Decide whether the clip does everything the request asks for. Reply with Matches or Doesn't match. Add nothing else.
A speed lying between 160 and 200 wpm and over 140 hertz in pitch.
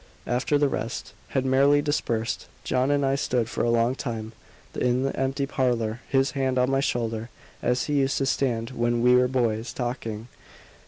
Doesn't match